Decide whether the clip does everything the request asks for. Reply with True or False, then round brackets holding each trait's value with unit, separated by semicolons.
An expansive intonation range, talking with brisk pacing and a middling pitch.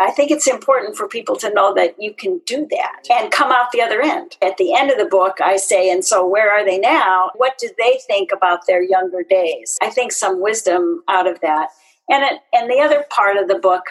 False (6.0 semitones; 245 wpm; 205 Hz)